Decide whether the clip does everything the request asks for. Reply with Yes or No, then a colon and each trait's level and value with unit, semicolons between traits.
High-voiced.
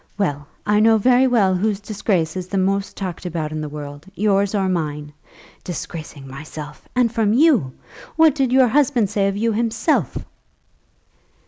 Yes: high, 195 Hz